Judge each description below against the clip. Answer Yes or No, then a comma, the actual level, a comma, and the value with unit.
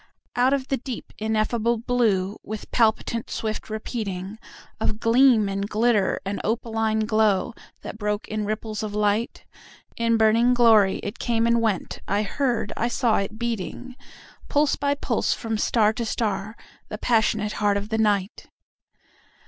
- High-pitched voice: Yes, high, 220 Hz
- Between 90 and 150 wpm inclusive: Yes, slow, 135 wpm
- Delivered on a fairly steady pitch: Yes, narrow, 2.0 semitones